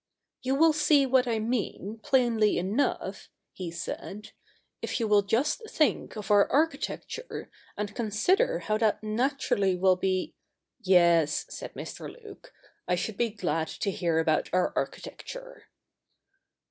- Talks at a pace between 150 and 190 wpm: Yes, average, 155 wpm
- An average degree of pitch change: No, wide, 6.5 semitones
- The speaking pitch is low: No, high, 215 Hz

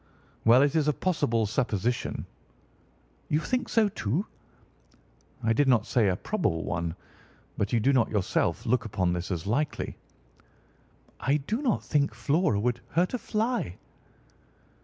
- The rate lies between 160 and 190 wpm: No, average, 145 wpm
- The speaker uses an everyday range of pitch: No, wide, 7.1 semitones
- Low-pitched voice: Yes, low, 125 Hz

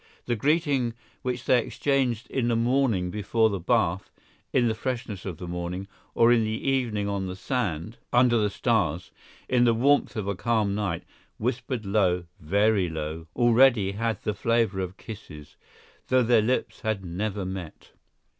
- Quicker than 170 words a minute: No, average, 165 wpm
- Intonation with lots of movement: No, average, 4.2 semitones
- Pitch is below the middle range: Yes, low, 110 Hz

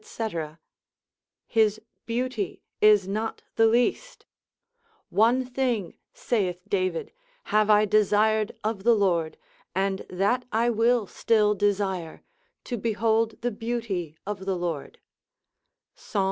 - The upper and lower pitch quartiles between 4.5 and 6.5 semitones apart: No, average, 3.0 semitones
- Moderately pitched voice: No, high, 210 Hz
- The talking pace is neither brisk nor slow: No, slow, 110 wpm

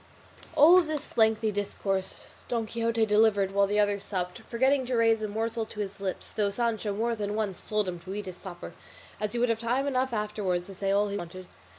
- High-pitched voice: Yes, high, 210 Hz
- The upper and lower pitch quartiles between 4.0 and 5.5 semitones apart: No, narrow, 2.6 semitones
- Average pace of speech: No, fast, 215 wpm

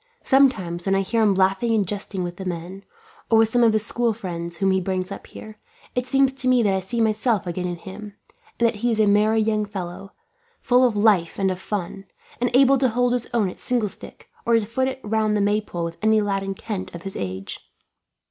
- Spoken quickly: Yes, fast, 230 wpm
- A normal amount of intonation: Yes, average, 3.4 semitones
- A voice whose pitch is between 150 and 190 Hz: No, high, 210 Hz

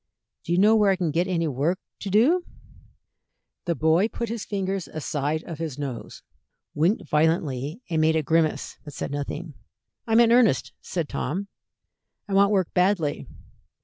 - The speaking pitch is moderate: Yes, medium, 170 Hz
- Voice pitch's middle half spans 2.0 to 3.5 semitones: No, average, 4.4 semitones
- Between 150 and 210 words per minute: Yes, average, 165 wpm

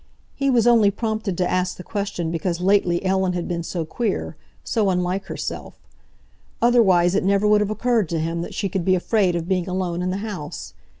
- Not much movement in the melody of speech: No, average, 3.0 semitones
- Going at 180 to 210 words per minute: Yes, average, 200 wpm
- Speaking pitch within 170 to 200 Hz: Yes, high, 190 Hz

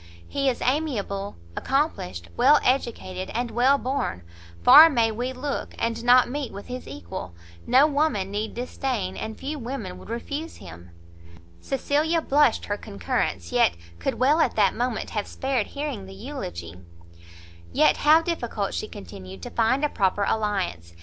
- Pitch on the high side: Yes, high, 235 Hz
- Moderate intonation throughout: No, wide, 6.3 semitones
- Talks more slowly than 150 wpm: No, average, 155 wpm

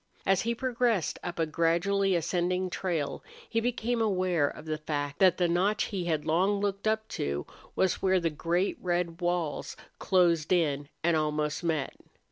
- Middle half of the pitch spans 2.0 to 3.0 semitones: No, average, 3.4 semitones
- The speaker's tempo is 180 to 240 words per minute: No, average, 165 wpm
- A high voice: No, medium, 175 Hz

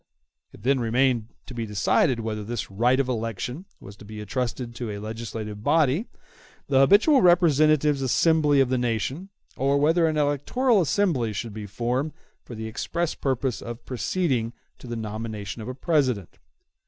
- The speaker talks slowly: No, average, 165 wpm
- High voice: No, low, 125 Hz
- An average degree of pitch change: Yes, average, 4.8 semitones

